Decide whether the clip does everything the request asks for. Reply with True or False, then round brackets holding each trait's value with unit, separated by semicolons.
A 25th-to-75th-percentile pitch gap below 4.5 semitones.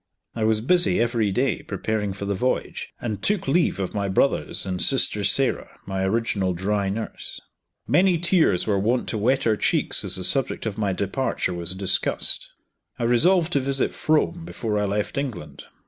False (5.5 semitones)